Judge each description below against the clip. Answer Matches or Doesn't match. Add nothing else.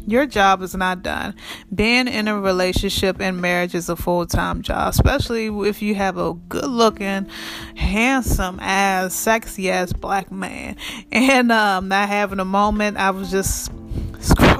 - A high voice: Matches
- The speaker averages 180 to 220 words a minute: Doesn't match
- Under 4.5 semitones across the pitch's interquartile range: Matches